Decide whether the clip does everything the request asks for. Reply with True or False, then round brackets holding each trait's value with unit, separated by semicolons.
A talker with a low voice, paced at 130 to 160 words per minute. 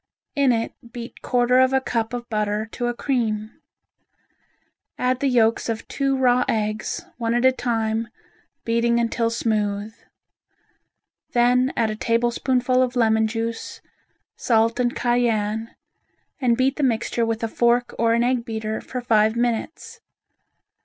False (235 Hz; 145 wpm)